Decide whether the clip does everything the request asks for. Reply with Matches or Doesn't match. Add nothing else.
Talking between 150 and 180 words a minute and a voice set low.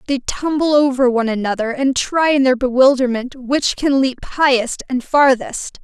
Doesn't match